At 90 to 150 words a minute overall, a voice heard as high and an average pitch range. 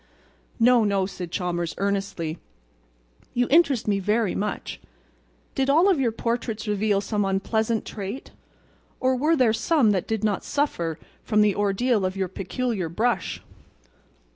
Yes: average, 140 wpm; high, 210 Hz; average, 4.0 semitones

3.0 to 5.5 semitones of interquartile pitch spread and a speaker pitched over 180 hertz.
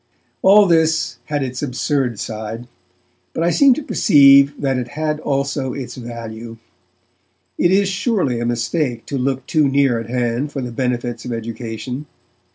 No: average, 3.9 semitones; low, 130 Hz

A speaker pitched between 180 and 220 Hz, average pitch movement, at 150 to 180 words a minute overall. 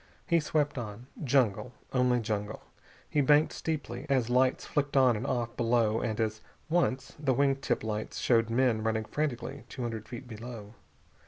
No: low, 125 Hz; average, 3.4 semitones; average, 165 wpm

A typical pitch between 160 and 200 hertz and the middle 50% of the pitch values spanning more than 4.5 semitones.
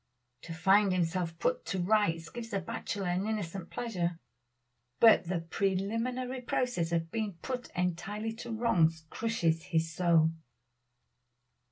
Yes: medium, 185 Hz; average, 5.0 semitones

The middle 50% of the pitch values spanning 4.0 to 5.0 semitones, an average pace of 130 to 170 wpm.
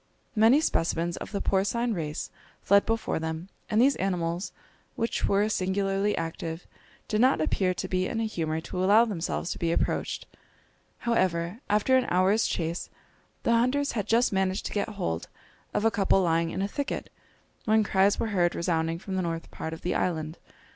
No: average, 4.4 semitones; average, 180 wpm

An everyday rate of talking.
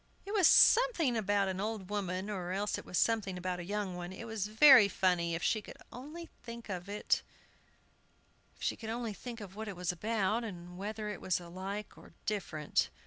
Yes: average, 165 wpm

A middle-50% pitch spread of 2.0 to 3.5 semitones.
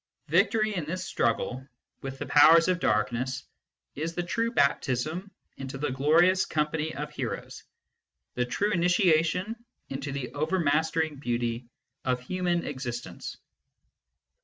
No: average, 5.1 semitones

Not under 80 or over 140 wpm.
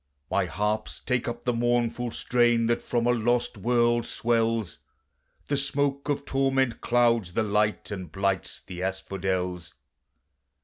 Yes: slow, 135 wpm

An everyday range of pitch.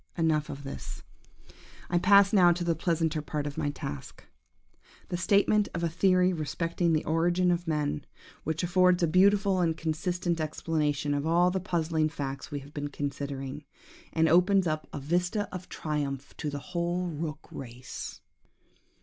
Yes: average, 3.2 semitones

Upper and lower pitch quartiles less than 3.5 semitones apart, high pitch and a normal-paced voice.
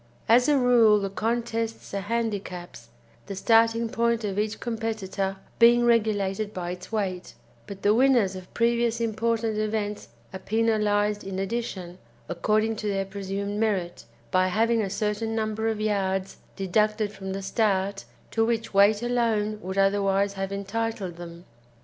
Yes: average, 2.7 semitones; high, 210 Hz; average, 150 wpm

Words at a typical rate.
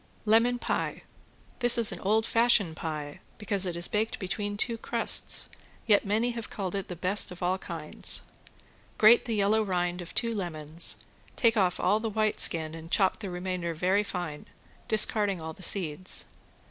Yes: average, 170 wpm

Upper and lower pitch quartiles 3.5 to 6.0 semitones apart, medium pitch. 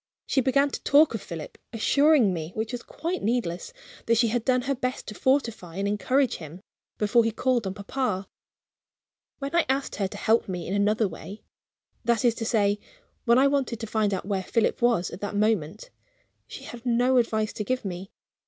No: average, 4.1 semitones; high, 225 Hz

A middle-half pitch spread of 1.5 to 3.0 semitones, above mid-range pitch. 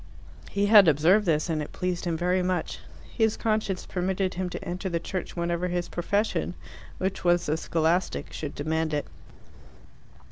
No: narrow, 2.5 semitones; medium, 180 Hz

